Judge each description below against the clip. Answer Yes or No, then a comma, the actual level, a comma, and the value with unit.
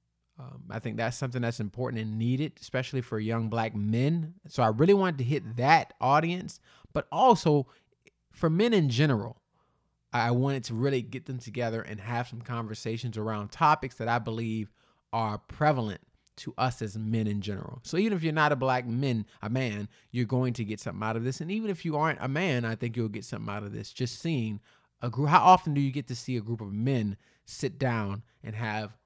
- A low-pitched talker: Yes, low, 120 Hz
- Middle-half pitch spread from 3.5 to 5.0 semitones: Yes, average, 4.5 semitones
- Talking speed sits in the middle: No, fast, 215 wpm